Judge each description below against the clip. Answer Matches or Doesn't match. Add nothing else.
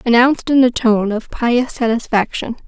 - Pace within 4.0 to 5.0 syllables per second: Matches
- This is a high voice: Matches